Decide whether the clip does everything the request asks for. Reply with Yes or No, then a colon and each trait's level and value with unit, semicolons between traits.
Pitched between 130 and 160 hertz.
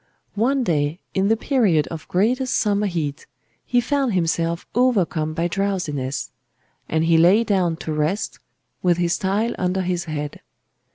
No: medium, 180 Hz